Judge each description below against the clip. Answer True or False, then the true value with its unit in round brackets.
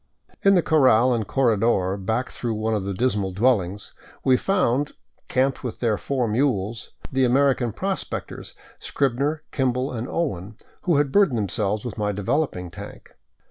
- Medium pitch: False (120 Hz)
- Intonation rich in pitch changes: False (4.5 semitones)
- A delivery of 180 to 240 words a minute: False (155 wpm)